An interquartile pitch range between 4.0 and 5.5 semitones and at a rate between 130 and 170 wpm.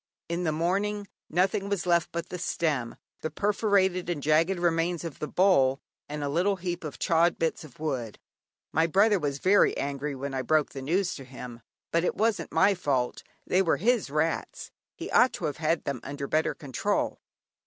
No: average, 4.5 semitones; average, 190 wpm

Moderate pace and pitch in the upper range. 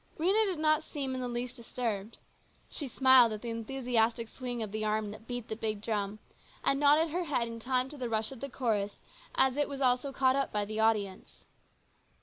No: fast, 210 wpm; high, 245 Hz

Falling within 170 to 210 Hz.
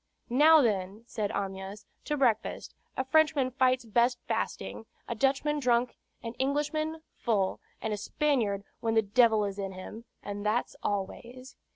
No: high, 235 Hz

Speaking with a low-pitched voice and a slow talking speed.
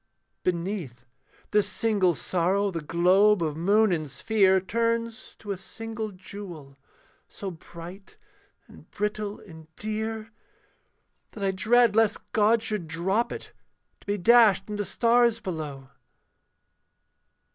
No: high, 200 Hz; slow, 120 wpm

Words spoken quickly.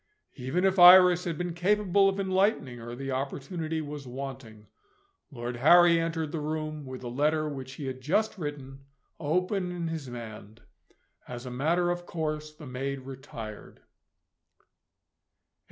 No: average, 145 wpm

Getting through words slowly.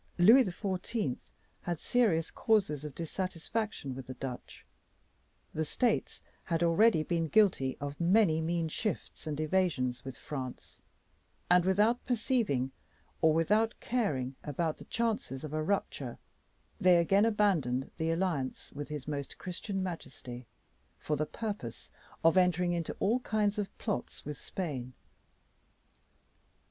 Yes: slow, 130 wpm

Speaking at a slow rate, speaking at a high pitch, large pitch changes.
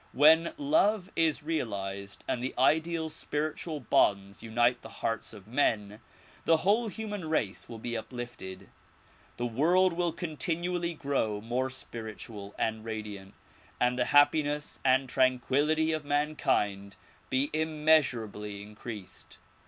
No: slow, 120 wpm; low, 130 Hz; wide, 6.3 semitones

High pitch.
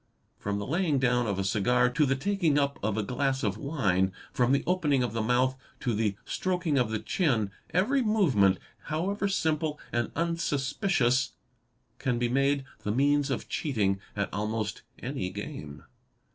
No: low, 130 Hz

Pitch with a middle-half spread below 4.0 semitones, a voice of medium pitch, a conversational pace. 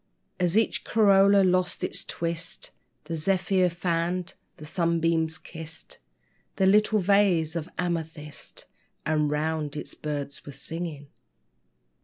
No: average, 2.8 semitones; medium, 170 Hz; slow, 115 wpm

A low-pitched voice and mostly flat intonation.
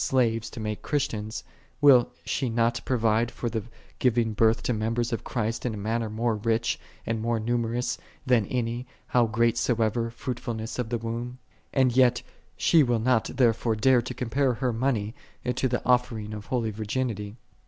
Yes: low, 115 Hz; narrow, 1.9 semitones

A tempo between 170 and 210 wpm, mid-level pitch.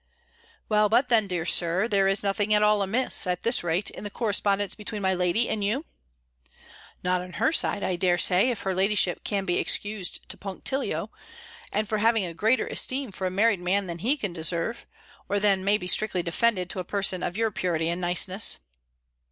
No: average, 200 wpm; high, 195 Hz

